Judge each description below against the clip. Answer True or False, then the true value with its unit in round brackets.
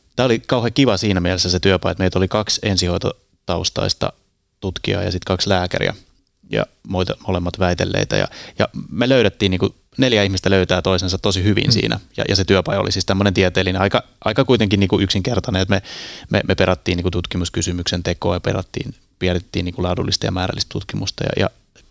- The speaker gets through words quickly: True (180 wpm)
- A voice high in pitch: False (95 Hz)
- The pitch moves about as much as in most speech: False (2.3 semitones)